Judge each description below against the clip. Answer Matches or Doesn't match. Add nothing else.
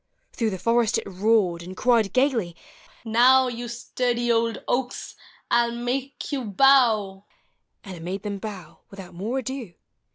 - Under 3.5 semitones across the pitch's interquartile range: Doesn't match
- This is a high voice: Matches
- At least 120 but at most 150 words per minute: Doesn't match